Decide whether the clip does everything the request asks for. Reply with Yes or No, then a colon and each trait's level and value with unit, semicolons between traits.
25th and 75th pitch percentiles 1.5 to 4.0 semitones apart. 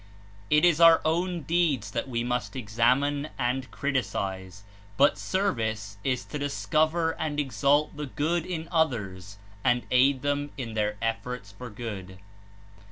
No: average, 5.3 semitones